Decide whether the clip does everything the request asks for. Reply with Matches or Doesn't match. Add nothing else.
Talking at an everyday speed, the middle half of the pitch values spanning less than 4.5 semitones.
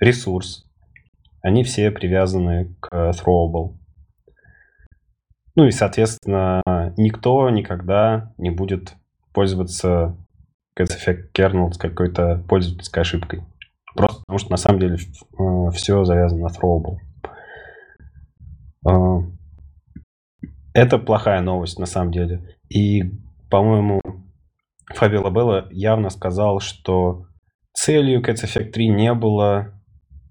Doesn't match